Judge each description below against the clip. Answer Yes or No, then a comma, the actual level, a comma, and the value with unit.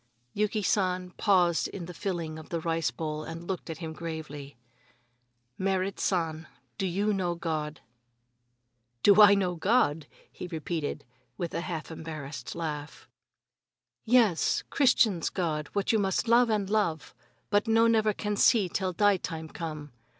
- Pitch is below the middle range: No, medium, 175 Hz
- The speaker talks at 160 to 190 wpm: No, average, 150 wpm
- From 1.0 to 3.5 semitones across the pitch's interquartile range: No, average, 4.2 semitones